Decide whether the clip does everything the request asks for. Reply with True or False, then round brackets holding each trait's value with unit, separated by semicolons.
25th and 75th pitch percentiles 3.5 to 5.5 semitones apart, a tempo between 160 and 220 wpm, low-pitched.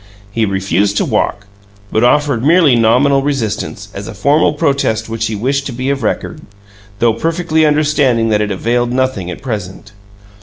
True (4.7 semitones; 165 wpm; 120 Hz)